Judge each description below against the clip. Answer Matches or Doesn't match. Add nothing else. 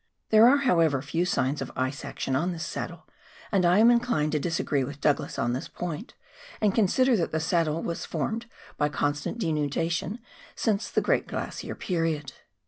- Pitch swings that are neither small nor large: Doesn't match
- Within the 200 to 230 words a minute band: Doesn't match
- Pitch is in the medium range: Matches